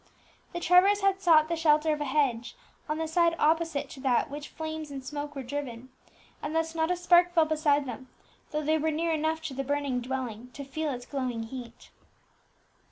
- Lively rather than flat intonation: No, average, 3.3 semitones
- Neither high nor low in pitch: No, very high, 300 Hz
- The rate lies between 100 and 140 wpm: No, fast, 205 wpm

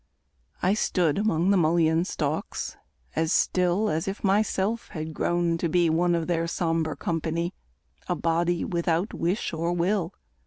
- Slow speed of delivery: No, average, 150 wpm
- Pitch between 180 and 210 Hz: No, medium, 170 Hz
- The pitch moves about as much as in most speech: No, narrow, 2.0 semitones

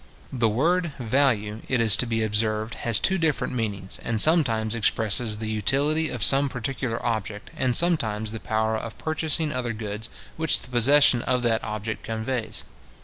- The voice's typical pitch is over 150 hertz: No, low, 115 Hz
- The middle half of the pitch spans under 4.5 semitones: Yes, average, 3.8 semitones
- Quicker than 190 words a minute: No, average, 165 wpm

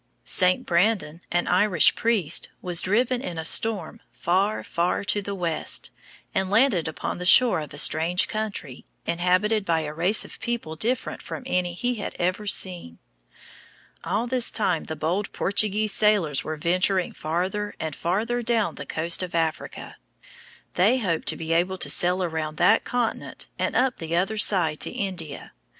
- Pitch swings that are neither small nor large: Yes, average, 4.1 semitones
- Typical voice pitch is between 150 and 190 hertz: Yes, medium, 185 Hz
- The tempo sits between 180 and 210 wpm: No, average, 165 wpm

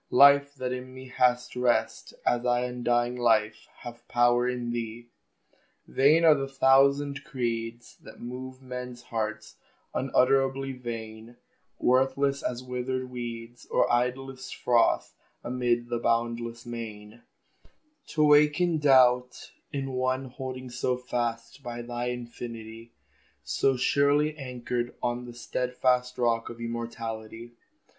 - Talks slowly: Yes, slow, 120 wpm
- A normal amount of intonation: No, narrow, 1.7 semitones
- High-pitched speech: No, low, 125 Hz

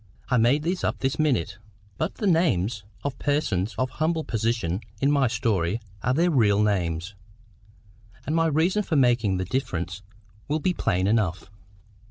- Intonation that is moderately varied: No, wide, 7.6 semitones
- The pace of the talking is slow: No, average, 165 wpm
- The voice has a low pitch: Yes, low, 120 Hz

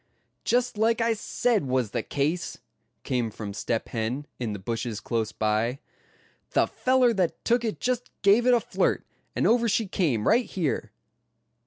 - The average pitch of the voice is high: No, medium, 165 Hz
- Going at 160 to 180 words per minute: Yes, average, 165 wpm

